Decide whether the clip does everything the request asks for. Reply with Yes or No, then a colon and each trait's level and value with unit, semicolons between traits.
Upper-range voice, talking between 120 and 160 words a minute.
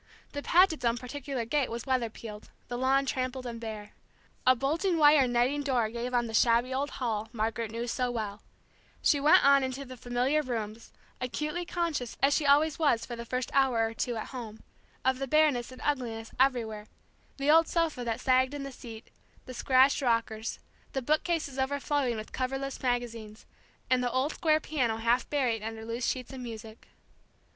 No: very high, 255 Hz; average, 185 wpm